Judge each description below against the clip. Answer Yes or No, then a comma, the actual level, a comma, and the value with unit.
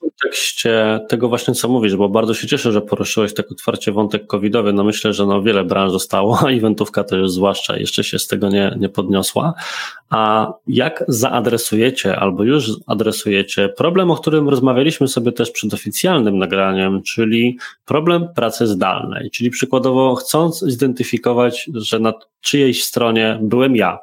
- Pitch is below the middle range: Yes, low, 115 Hz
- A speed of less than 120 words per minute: No, fast, 160 wpm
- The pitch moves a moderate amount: Yes, average, 3.7 semitones